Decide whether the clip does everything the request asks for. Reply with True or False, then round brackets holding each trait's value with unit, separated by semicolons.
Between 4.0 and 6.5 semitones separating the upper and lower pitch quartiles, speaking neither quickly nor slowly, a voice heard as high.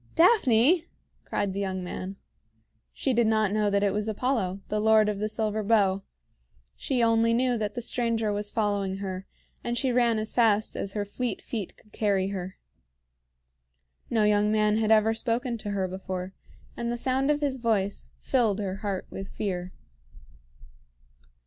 False (2.8 semitones; 170 wpm; 215 Hz)